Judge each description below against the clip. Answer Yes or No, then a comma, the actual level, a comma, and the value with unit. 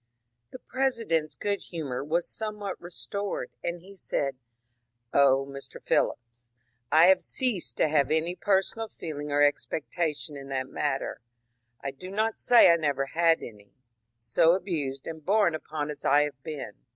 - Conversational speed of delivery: Yes, average, 165 wpm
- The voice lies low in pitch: No, medium, 155 Hz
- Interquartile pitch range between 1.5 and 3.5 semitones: No, average, 4.9 semitones